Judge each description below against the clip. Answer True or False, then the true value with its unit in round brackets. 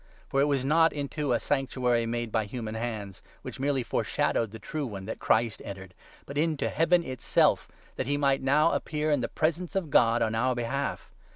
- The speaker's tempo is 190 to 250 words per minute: True (200 wpm)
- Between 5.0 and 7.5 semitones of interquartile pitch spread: False (4.2 semitones)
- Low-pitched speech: True (130 Hz)